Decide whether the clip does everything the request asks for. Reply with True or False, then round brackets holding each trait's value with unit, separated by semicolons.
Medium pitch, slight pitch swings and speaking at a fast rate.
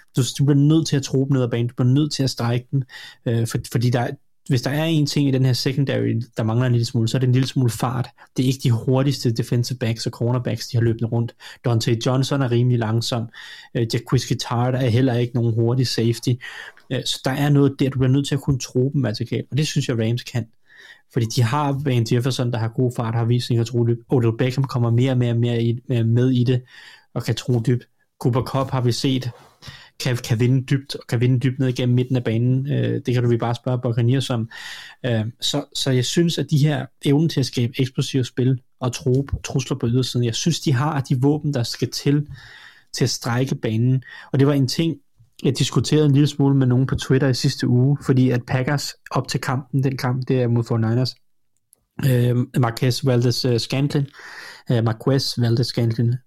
False (130 Hz; 2.3 semitones; 235 wpm)